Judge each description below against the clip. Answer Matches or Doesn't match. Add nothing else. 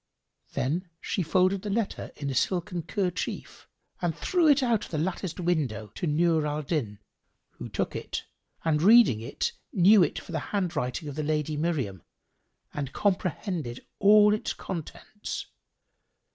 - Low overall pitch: Doesn't match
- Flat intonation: Doesn't match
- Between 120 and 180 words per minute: Matches